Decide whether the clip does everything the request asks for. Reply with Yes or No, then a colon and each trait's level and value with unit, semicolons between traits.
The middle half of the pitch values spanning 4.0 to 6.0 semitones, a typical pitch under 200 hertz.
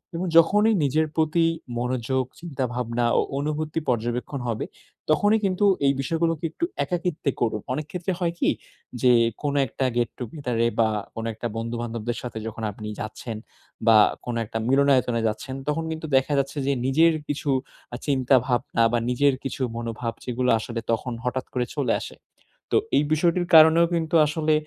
Yes: average, 4.9 semitones; low, 135 Hz